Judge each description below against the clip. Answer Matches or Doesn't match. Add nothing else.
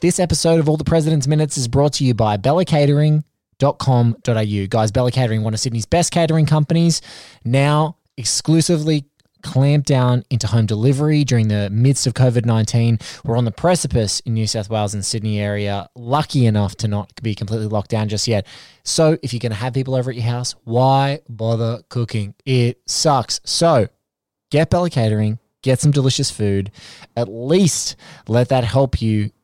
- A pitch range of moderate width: Matches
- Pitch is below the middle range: Matches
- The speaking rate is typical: Matches